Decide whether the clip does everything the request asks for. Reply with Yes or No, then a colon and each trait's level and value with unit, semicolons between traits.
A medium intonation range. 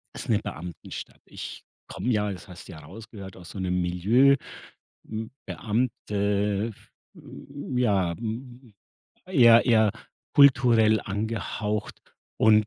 Yes: average, 3.2 semitones